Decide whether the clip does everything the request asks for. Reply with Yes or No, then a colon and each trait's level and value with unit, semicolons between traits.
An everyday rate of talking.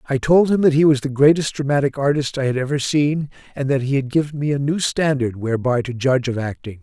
No: fast, 245 wpm